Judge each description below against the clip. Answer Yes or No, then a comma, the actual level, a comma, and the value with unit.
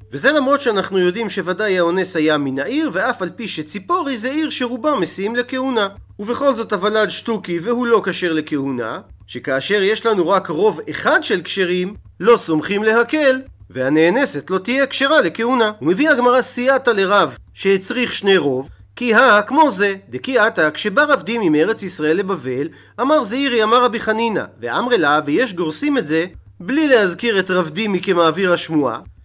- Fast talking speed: Yes, fast, 160 wpm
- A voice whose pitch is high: Yes, high, 205 Hz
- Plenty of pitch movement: Yes, wide, 6.4 semitones